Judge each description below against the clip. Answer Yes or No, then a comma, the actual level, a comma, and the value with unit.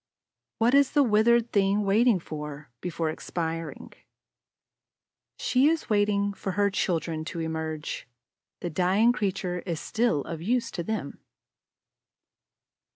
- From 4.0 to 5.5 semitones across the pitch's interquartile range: Yes, average, 5.2 semitones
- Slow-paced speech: Yes, slow, 120 wpm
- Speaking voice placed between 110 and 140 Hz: No, high, 195 Hz